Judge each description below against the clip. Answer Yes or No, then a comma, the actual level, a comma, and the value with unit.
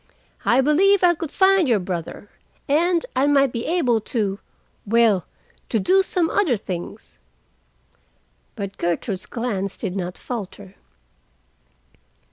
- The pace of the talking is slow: Yes, slow, 115 wpm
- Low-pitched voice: No, high, 235 Hz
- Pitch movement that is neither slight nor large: No, wide, 8.8 semitones